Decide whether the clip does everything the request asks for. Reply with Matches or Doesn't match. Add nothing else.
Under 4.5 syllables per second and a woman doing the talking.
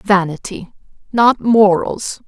Matches